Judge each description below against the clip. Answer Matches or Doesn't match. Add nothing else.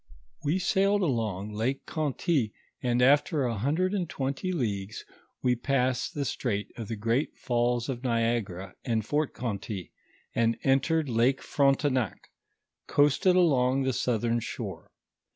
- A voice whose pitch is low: Matches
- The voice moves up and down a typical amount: Matches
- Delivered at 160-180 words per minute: Doesn't match